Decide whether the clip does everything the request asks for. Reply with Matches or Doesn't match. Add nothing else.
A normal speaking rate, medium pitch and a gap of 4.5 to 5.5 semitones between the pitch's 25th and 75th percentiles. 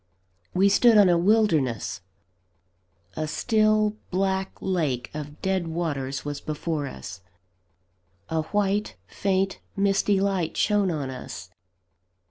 Doesn't match